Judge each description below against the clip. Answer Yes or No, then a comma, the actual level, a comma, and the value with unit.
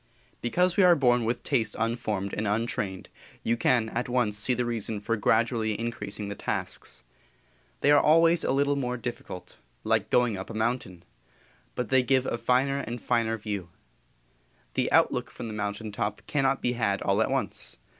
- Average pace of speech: Yes, average, 175 wpm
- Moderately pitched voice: No, low, 115 Hz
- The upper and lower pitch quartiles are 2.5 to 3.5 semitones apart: Yes, average, 3.1 semitones